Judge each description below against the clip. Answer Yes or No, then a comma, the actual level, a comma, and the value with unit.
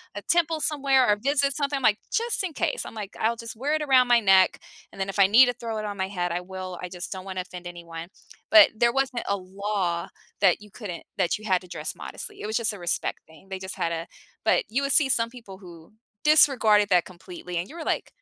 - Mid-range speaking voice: No, high, 210 Hz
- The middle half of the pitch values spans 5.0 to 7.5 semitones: Yes, wide, 5.6 semitones